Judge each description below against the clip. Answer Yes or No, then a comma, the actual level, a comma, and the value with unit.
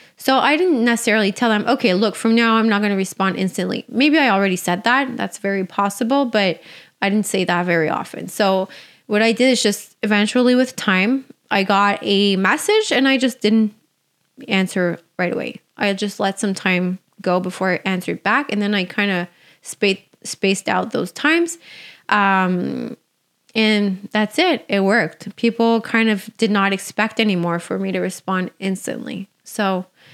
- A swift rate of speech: No, average, 180 wpm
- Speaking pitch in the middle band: No, high, 205 Hz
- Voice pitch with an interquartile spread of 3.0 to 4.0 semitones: Yes, average, 3.5 semitones